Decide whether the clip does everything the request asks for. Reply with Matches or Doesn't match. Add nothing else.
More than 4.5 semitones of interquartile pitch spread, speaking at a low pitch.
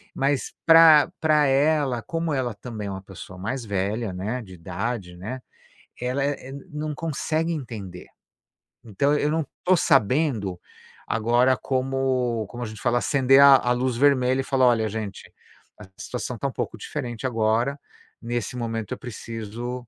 Doesn't match